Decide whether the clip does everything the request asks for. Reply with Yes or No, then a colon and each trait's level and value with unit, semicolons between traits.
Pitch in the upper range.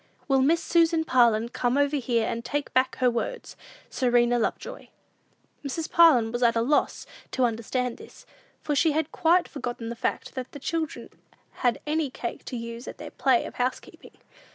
Yes: very high, 255 Hz